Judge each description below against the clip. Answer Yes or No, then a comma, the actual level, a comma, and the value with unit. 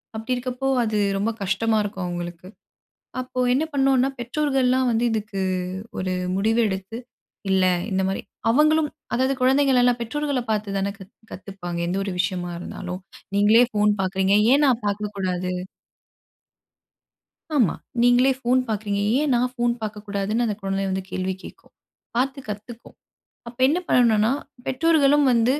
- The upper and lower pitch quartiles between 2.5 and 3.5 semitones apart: No, average, 4.7 semitones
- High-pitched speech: Yes, high, 225 Hz